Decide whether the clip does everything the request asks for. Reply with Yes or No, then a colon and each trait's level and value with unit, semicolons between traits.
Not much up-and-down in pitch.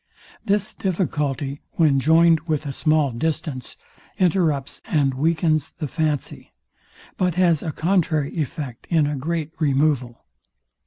No: average, 3.0 semitones